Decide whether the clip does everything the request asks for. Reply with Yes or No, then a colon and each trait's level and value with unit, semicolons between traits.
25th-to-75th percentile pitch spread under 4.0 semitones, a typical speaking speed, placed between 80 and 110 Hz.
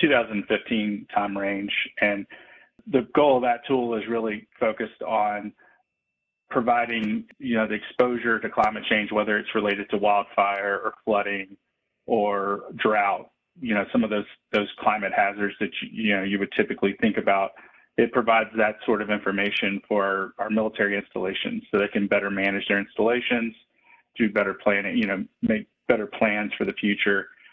Yes: narrow, 2.4 semitones; average, 165 wpm; low, 105 Hz